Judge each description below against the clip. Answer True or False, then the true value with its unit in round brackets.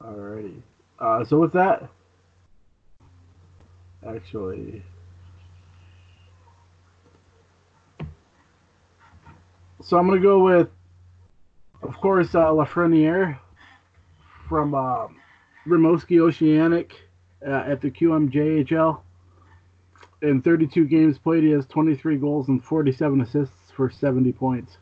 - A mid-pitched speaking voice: False (105 Hz)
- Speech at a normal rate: False (90 wpm)